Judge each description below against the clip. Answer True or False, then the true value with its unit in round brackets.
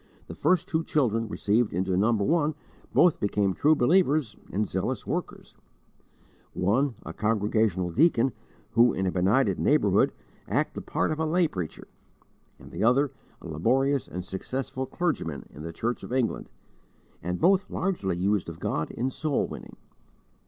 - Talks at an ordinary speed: True (155 wpm)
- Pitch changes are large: True (7.4 semitones)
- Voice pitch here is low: True (115 Hz)